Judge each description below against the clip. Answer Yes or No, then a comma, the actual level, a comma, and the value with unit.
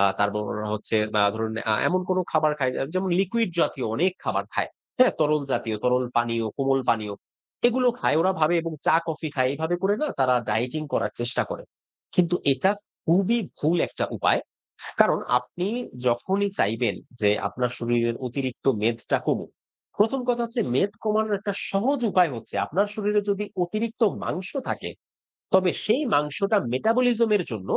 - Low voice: No, medium, 160 Hz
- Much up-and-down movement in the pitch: Yes, wide, 8.6 semitones